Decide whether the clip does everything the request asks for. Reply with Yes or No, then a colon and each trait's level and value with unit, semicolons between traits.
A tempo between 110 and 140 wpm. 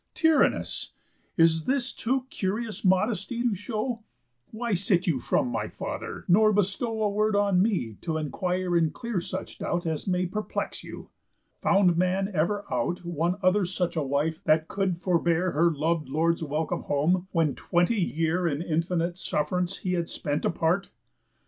No: average, 160 wpm